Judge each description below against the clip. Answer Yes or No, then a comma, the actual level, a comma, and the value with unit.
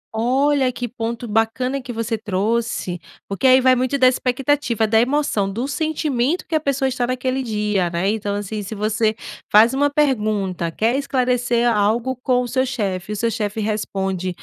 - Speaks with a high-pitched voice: Yes, high, 235 Hz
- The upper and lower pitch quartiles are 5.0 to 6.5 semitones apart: No, average, 3.6 semitones